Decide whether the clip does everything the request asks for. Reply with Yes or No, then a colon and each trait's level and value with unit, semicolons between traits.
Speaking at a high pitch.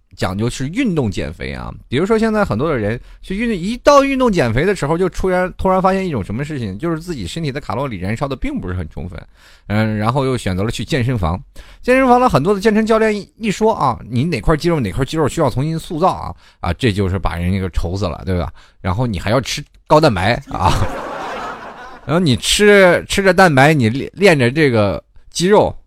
No: medium, 140 Hz